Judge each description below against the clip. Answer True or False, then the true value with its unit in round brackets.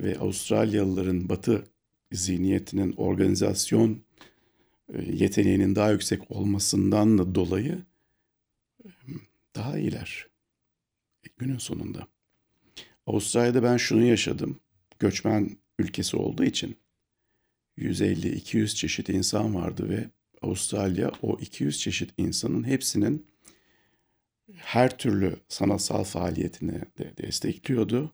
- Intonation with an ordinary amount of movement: True (3.4 semitones)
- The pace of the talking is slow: True (85 wpm)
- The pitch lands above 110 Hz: False (105 Hz)